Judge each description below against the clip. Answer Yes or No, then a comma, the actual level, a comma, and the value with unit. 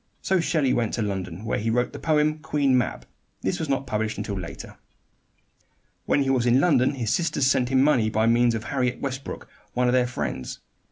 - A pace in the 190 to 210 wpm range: Yes, fast, 205 wpm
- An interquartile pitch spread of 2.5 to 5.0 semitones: Yes, average, 3.6 semitones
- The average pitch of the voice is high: No, low, 125 Hz